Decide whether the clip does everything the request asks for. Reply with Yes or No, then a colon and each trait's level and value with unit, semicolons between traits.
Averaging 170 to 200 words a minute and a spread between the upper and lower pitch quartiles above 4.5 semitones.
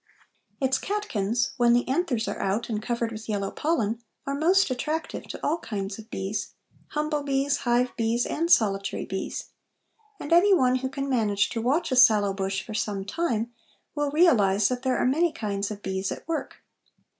Yes: average, 180 wpm; wide, 5.6 semitones